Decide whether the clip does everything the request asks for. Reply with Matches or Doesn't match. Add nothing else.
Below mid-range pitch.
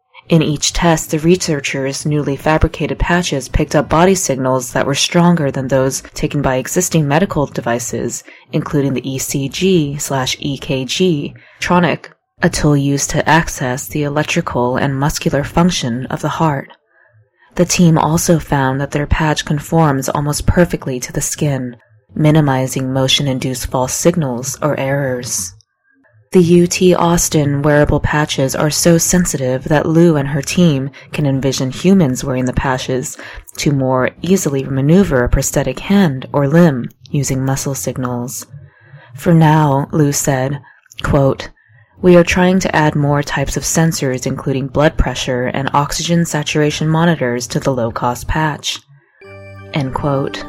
Doesn't match